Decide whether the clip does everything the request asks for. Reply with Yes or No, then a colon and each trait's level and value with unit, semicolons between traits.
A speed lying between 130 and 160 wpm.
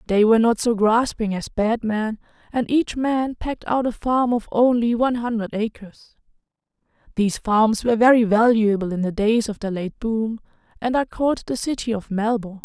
No: average, 180 wpm